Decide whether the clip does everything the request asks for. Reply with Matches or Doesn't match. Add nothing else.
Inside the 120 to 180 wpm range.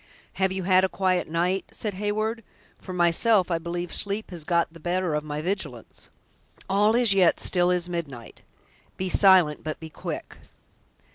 Matches